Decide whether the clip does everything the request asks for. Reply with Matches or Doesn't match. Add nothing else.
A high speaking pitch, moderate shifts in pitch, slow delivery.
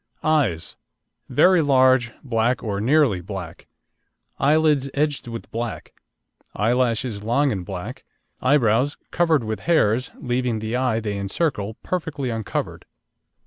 Doesn't match